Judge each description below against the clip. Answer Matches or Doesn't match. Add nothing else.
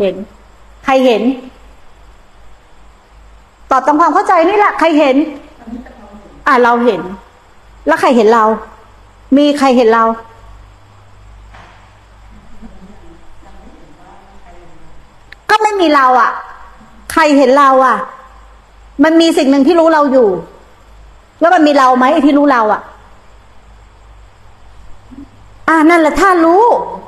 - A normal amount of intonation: Doesn't match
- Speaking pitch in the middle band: Doesn't match